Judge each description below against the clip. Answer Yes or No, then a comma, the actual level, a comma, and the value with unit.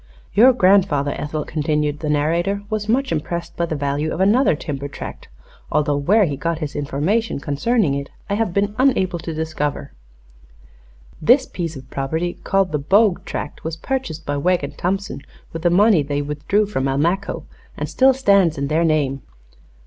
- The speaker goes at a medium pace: Yes, average, 170 wpm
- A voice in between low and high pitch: Yes, medium, 165 Hz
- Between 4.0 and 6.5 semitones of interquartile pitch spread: Yes, wide, 5.4 semitones